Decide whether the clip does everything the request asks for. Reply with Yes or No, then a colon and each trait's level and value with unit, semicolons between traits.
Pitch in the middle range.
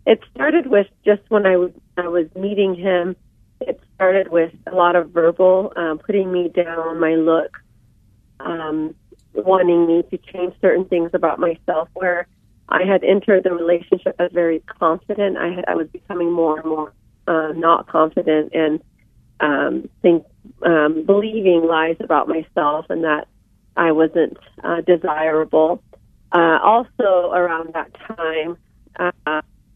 Yes: medium, 170 Hz